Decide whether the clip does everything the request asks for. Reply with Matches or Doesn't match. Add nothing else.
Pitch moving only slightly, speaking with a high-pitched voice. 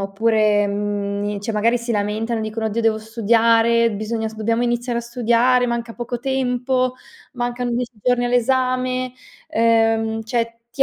Matches